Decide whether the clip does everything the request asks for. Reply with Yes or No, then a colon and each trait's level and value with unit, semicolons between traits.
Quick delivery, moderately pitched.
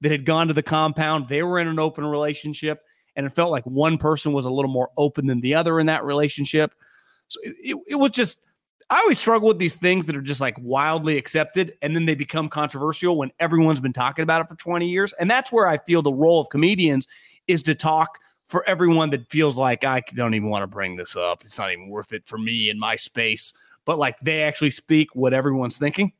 Yes: fast, 235 wpm; medium, 155 Hz